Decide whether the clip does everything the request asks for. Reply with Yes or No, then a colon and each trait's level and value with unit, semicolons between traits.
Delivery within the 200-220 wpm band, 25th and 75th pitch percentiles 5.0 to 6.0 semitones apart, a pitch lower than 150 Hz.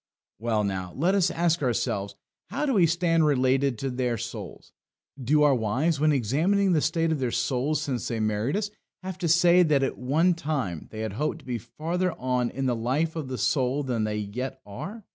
Yes: fast, 205 wpm; wide, 5.5 semitones; low, 135 Hz